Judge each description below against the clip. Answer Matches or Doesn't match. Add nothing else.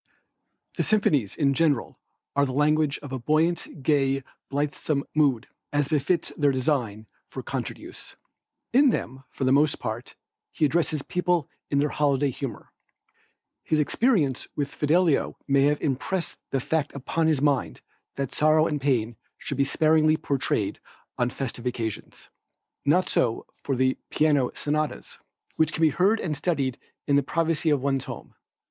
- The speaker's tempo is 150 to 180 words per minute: Matches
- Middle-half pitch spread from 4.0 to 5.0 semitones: Doesn't match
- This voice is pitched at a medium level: Matches